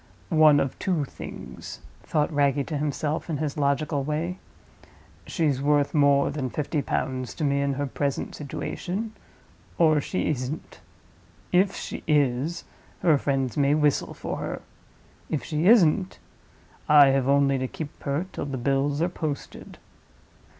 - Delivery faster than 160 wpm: No, average, 145 wpm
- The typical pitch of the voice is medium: Yes, medium, 145 Hz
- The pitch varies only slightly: Yes, narrow, 2.1 semitones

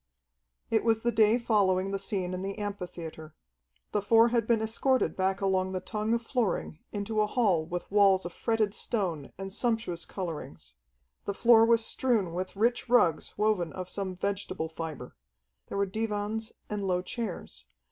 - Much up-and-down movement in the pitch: No, average, 3.4 semitones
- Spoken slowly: No, average, 165 wpm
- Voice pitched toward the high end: Yes, high, 200 Hz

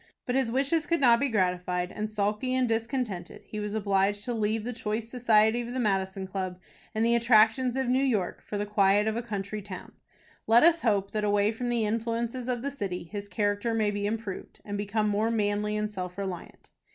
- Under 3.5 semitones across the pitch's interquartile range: Yes, narrow, 2.6 semitones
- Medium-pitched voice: No, high, 215 Hz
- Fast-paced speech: Yes, fast, 210 wpm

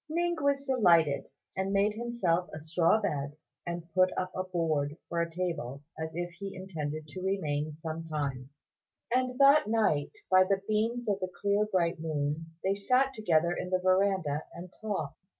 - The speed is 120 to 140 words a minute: No, average, 170 wpm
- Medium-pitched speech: Yes, medium, 180 Hz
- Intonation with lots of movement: No, average, 4.3 semitones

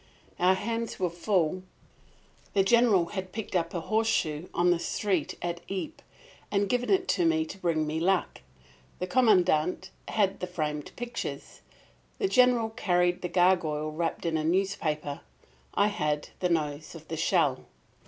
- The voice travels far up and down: No, average, 4.6 semitones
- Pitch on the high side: No, medium, 180 Hz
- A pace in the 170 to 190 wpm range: No, average, 155 wpm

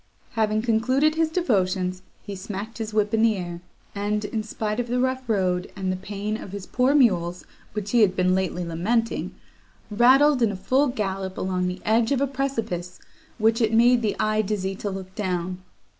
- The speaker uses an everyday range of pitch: Yes, average, 3.9 semitones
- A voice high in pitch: Yes, high, 210 Hz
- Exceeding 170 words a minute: Yes, average, 190 wpm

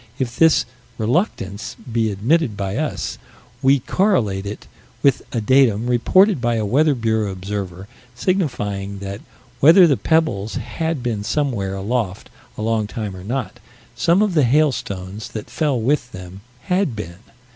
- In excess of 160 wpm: No, average, 145 wpm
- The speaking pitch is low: Yes, low, 115 Hz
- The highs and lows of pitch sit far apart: Yes, wide, 6.4 semitones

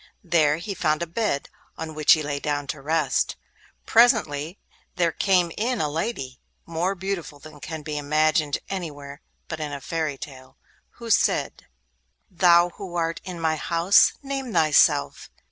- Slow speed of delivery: No, average, 155 wpm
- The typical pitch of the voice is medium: Yes, medium, 160 Hz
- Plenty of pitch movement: No, average, 3.5 semitones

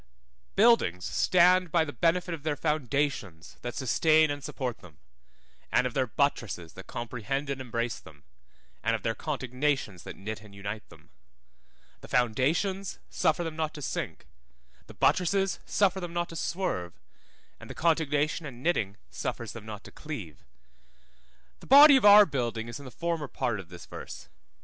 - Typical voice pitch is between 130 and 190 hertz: Yes, medium, 140 Hz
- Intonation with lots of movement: Yes, wide, 7.1 semitones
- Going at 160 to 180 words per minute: Yes, average, 165 wpm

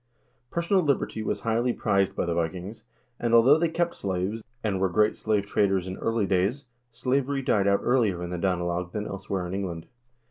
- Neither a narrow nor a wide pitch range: Yes, average, 4.4 semitones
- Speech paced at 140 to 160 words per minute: No, average, 185 wpm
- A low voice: Yes, low, 100 Hz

